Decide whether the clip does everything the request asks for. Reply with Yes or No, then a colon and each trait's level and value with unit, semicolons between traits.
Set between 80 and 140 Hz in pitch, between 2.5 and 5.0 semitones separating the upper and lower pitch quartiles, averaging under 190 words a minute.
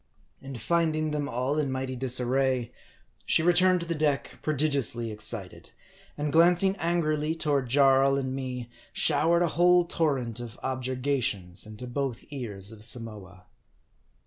Yes: low, 135 Hz; average, 4.3 semitones; slow, 135 wpm